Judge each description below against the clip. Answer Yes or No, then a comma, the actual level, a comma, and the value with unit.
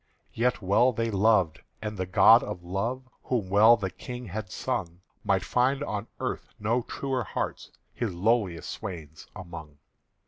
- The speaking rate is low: No, average, 160 wpm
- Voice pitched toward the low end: Yes, low, 105 Hz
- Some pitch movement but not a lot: Yes, average, 4.4 semitones